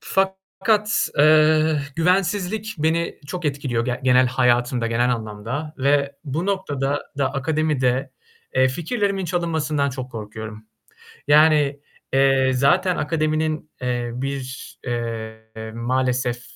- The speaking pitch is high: No, medium, 140 Hz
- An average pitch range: Yes, average, 4.2 semitones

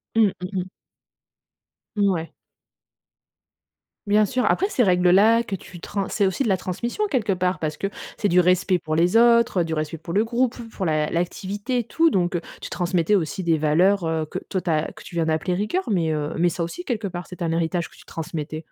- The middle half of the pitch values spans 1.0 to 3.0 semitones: No, average, 3.8 semitones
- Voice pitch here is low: No, medium, 180 Hz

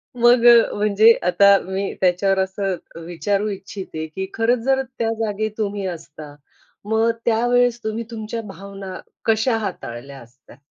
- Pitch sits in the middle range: No, high, 205 Hz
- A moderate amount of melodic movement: Yes, average, 3.1 semitones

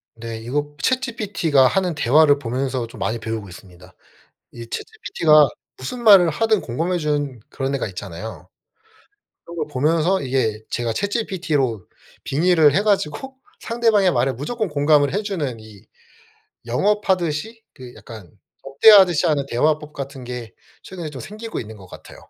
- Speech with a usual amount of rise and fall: No, wide, 7.6 semitones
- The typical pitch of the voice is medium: Yes, medium, 145 Hz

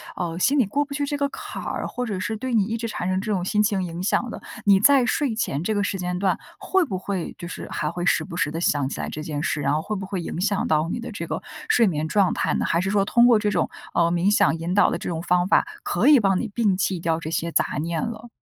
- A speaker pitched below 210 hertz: Yes, high, 190 Hz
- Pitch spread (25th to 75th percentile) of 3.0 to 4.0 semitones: No, average, 4.5 semitones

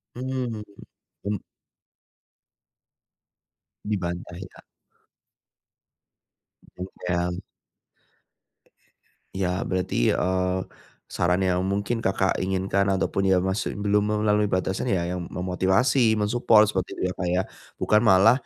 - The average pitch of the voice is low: Yes, very low, 95 Hz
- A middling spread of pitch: No, narrow, 2.3 semitones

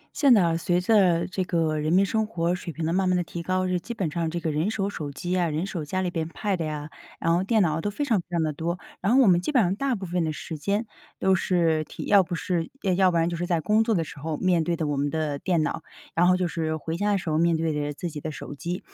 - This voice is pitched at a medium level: Yes, medium, 175 Hz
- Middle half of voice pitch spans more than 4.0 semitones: No, average, 2.8 semitones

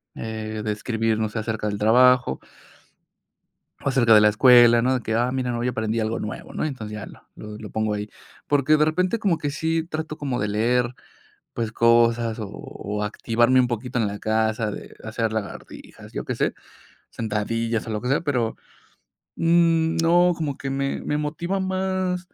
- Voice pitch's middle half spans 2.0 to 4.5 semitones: No, average, 5.1 semitones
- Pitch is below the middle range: Yes, low, 120 Hz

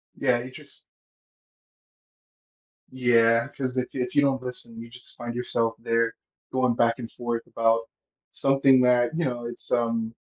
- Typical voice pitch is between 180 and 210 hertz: No, low, 120 Hz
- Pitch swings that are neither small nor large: No, narrow, 1.7 semitones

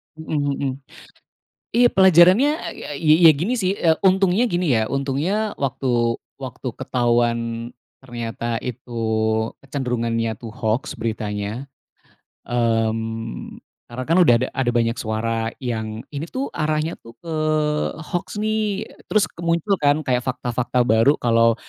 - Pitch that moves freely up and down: Yes, wide, 6.3 semitones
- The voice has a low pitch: Yes, low, 125 Hz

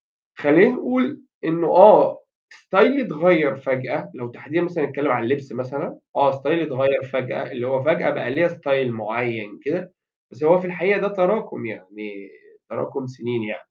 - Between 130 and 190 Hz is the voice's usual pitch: Yes, medium, 140 Hz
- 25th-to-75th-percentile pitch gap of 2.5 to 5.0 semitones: No, wide, 5.6 semitones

